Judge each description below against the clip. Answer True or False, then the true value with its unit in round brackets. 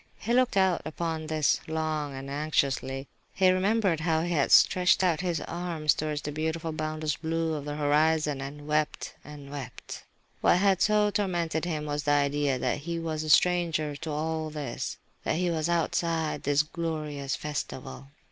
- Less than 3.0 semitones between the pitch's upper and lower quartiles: True (2.4 semitones)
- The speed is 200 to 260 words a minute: False (170 wpm)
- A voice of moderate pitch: True (155 Hz)